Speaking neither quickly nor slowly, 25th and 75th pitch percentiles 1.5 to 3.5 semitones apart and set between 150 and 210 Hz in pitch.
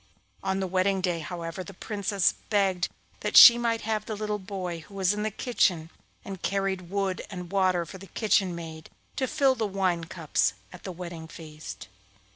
Yes: average, 185 wpm; average, 2.8 semitones; high, 190 Hz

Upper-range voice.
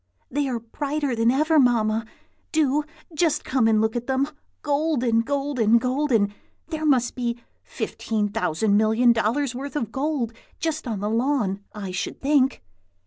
Yes: very high, 250 Hz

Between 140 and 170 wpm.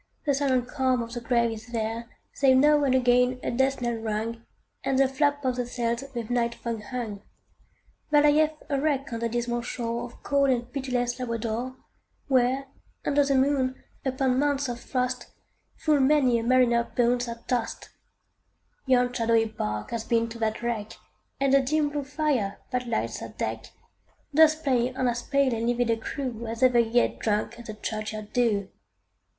No: average, 180 wpm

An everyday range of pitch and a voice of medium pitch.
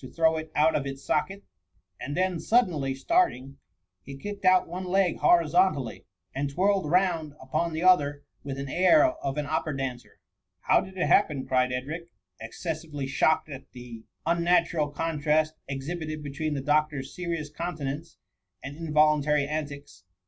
Yes: average, 3.6 semitones; medium, 155 Hz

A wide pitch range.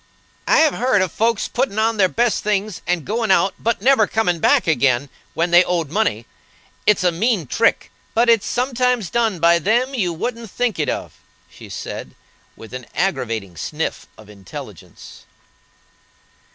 Yes: wide, 5.8 semitones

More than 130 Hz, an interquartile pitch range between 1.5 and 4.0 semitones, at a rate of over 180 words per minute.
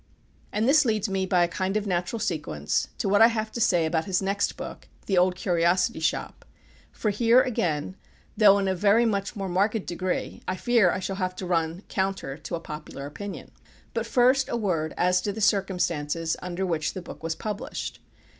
Yes: high, 190 Hz; average, 3.5 semitones; average, 200 wpm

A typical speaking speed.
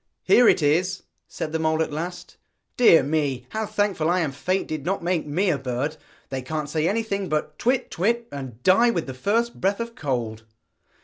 Yes: average, 195 wpm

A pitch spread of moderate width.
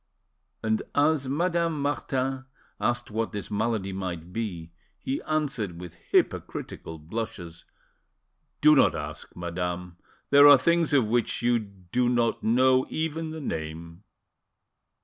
No: wide, 8.0 semitones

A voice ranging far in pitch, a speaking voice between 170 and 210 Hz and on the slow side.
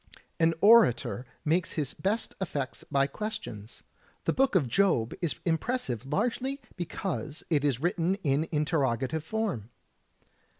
No: wide, 6.5 semitones; medium, 160 Hz; slow, 130 wpm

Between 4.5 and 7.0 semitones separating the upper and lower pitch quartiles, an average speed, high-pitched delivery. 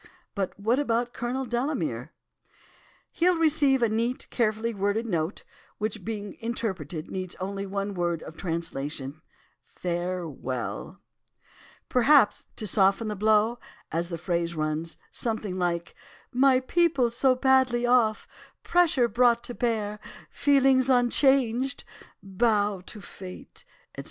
No: average, 5.2 semitones; slow, 115 wpm; high, 220 Hz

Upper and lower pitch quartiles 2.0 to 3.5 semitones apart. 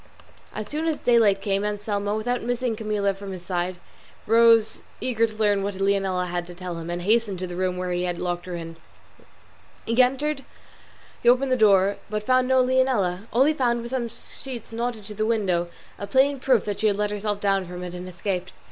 No: average, 4.3 semitones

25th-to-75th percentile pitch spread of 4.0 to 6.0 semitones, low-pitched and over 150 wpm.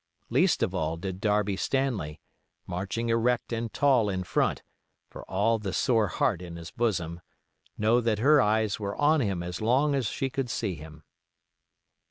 Yes: average, 4.6 semitones; low, 105 Hz; average, 170 wpm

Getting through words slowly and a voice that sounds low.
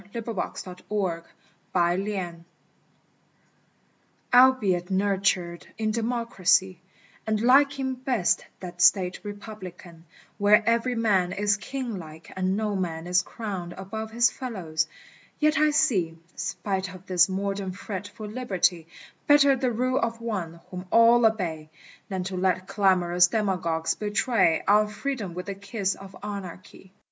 No: slow, 125 wpm; high, 200 Hz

